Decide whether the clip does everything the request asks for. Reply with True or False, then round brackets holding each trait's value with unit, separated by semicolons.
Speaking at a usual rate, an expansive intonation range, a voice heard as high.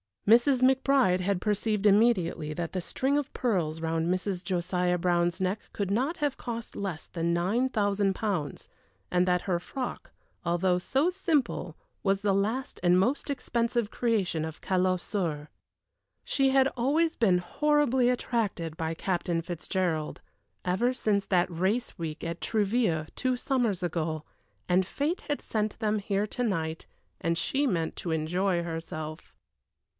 True (150 wpm; 5.7 semitones; 195 Hz)